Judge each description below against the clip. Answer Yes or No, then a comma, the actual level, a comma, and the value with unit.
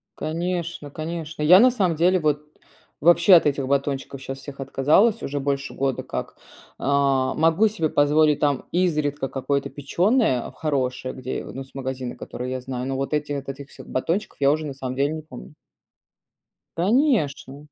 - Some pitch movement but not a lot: Yes, average, 3.5 semitones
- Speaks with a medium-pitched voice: Yes, medium, 145 Hz